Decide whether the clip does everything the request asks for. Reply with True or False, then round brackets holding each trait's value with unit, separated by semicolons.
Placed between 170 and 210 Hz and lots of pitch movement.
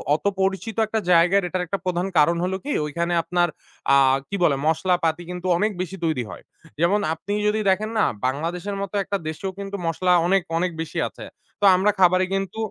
False (185 Hz; 2.6 semitones)